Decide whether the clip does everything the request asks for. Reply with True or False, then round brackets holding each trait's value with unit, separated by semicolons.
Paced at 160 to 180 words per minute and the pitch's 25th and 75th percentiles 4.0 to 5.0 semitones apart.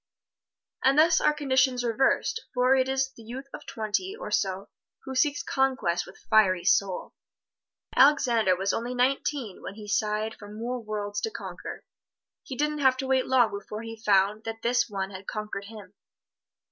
True (170 wpm; 4.4 semitones)